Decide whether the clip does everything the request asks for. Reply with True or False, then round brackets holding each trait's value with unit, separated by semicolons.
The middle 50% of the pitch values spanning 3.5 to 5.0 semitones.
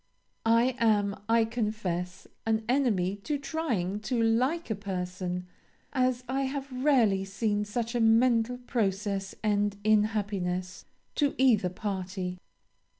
True (4.2 semitones)